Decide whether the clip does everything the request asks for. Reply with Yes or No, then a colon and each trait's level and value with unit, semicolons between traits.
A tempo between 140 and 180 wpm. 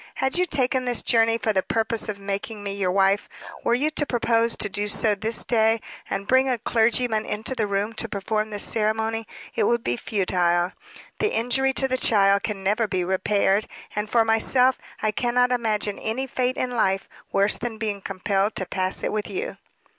No: average, 195 wpm